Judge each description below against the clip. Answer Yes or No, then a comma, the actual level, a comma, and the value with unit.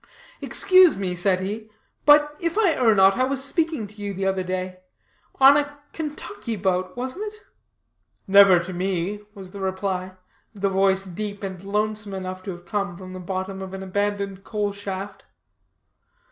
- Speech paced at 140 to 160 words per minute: No, average, 170 wpm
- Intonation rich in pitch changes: No, average, 3.0 semitones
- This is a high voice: Yes, high, 195 Hz